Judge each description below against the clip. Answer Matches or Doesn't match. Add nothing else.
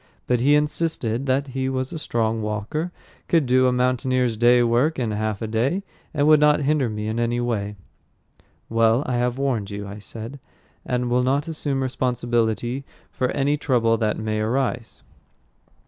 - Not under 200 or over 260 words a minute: Doesn't match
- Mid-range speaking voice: Doesn't match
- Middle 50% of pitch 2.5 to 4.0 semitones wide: Matches